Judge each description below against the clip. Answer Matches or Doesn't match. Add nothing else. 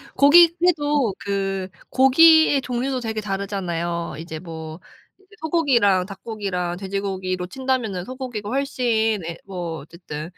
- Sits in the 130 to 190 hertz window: Doesn't match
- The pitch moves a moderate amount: Doesn't match